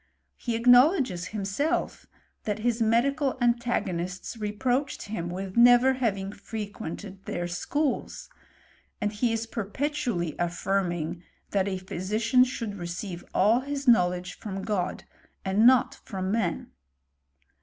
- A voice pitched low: No, high, 210 Hz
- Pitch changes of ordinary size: Yes, average, 4.6 semitones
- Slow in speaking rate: Yes, slow, 115 wpm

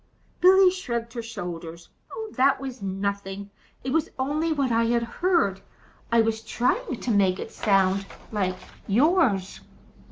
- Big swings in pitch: Yes, wide, 5.7 semitones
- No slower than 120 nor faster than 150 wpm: Yes, slow, 135 wpm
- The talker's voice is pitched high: Yes, high, 230 Hz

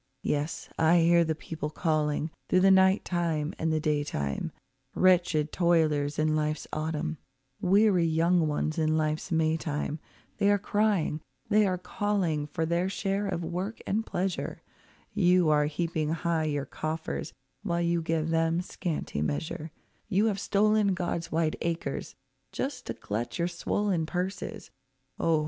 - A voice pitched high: No, medium, 165 Hz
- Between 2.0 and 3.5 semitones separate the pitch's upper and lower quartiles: Yes, average, 2.9 semitones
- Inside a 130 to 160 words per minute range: Yes, average, 150 wpm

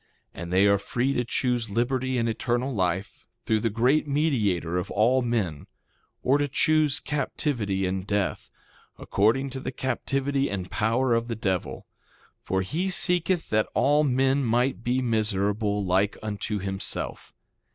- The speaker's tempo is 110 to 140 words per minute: No, average, 150 wpm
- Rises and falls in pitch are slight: No, average, 4.9 semitones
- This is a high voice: No, low, 115 Hz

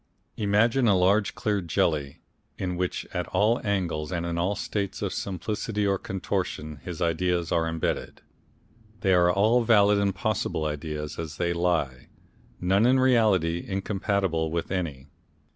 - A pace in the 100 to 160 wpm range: Yes, average, 145 wpm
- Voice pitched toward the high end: No, very low, 90 Hz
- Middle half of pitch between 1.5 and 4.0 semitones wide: Yes, average, 3.6 semitones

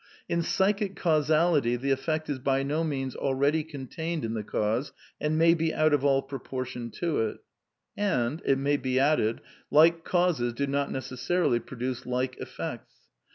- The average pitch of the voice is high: No, medium, 140 Hz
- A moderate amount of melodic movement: Yes, average, 3.8 semitones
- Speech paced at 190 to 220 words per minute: No, average, 175 wpm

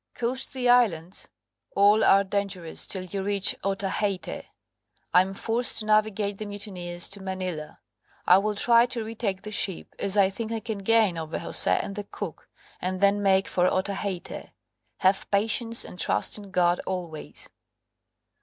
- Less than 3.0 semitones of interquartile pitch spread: Yes, narrow, 2.4 semitones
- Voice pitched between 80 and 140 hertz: No, high, 200 Hz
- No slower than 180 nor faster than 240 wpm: No, average, 155 wpm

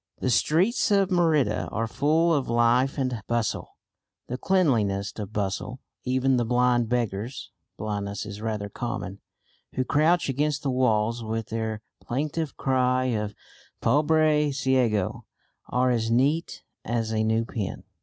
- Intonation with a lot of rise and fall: No, average, 4.3 semitones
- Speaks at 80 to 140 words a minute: Yes, slow, 135 wpm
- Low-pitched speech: Yes, low, 125 Hz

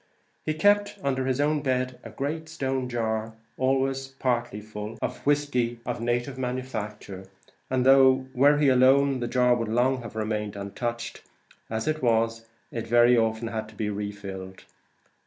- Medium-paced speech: Yes, average, 165 wpm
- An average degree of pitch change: Yes, average, 3.1 semitones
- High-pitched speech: No, low, 125 Hz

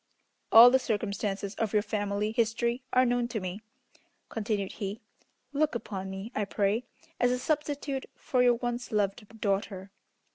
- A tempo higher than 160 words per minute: No, average, 150 wpm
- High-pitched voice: Yes, high, 220 Hz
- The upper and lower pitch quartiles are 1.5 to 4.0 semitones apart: Yes, average, 3.4 semitones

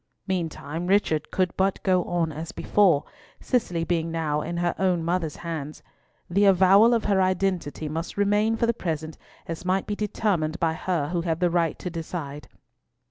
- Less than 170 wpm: No, average, 175 wpm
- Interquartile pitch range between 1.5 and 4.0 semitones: Yes, average, 2.9 semitones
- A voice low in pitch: No, medium, 175 Hz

